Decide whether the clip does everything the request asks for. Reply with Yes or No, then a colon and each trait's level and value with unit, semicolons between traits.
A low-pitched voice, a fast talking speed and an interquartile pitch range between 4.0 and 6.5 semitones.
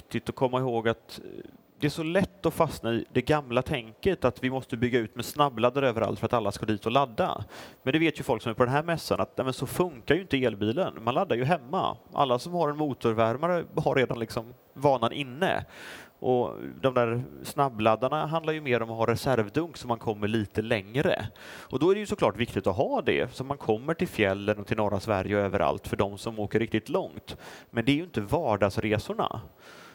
Yes: low, 125 Hz; fast, 220 wpm; average, 4.4 semitones